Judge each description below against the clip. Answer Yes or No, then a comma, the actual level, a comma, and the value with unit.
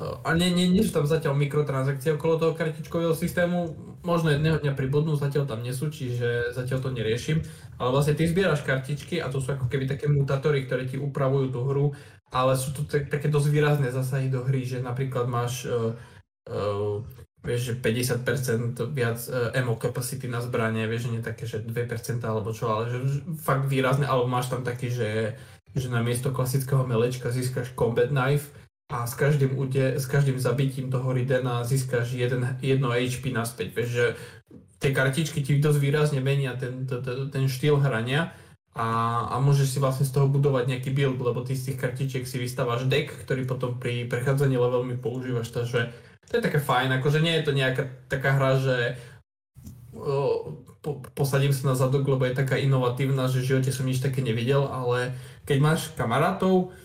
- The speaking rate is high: Yes, fast, 185 wpm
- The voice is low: Yes, low, 130 Hz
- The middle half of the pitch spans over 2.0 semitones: Yes, average, 2.7 semitones